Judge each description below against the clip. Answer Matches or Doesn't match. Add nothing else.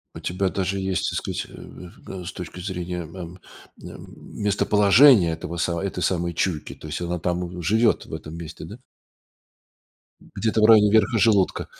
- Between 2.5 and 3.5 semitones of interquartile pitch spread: Matches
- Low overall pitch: Matches